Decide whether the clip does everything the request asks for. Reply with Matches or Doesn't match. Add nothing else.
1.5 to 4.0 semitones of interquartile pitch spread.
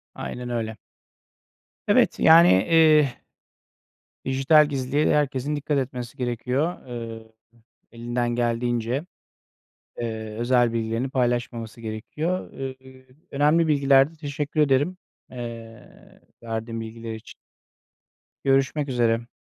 Matches